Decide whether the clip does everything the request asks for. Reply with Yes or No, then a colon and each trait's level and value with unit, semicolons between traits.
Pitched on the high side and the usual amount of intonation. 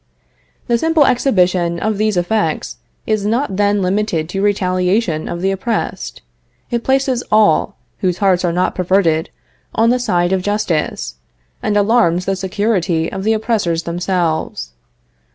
Yes: high, 195 Hz; average, 3.7 semitones